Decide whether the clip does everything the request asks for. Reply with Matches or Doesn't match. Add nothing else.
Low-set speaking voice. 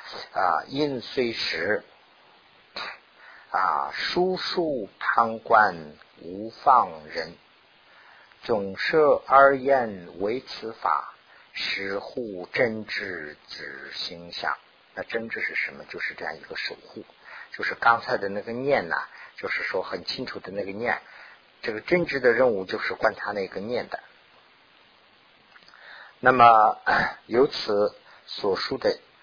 Doesn't match